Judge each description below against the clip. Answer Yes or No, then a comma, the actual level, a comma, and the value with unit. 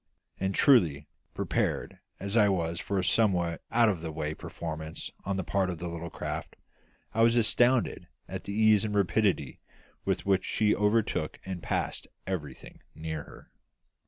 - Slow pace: No, average, 160 wpm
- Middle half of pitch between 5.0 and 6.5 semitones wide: No, average, 4.3 semitones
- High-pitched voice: No, very low, 95 Hz